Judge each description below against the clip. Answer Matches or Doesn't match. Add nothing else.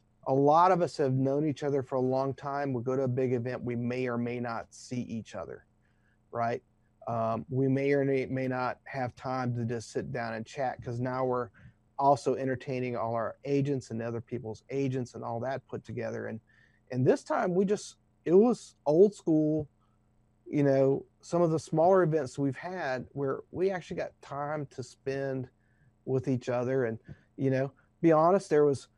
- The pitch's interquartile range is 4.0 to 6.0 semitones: Doesn't match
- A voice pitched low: Matches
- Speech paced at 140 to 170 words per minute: Doesn't match